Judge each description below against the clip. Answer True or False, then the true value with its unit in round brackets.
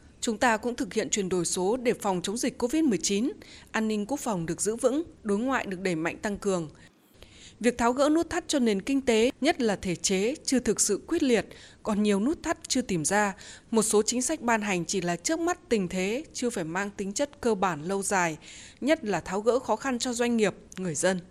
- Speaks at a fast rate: False (235 wpm)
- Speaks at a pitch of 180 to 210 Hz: False (220 Hz)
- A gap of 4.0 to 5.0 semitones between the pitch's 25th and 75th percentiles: True (4.6 semitones)